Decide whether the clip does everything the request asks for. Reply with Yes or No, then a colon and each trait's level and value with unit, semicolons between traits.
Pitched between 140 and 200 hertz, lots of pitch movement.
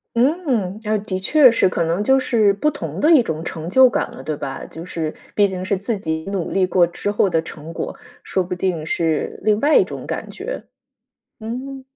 Yes: high, 195 Hz; wide, 6.3 semitones